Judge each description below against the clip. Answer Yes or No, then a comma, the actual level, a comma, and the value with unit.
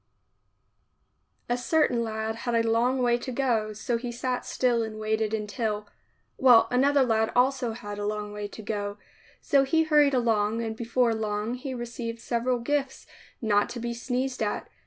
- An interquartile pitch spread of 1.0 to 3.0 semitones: Yes, narrow, 2.4 semitones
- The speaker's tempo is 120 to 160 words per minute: No, average, 180 wpm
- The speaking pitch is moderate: No, high, 235 Hz